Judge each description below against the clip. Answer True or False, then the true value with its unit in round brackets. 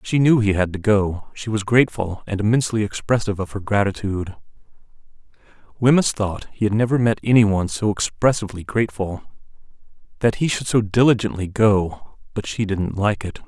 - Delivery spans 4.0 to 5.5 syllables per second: False (5.7 syllables/s)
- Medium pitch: False (105 Hz)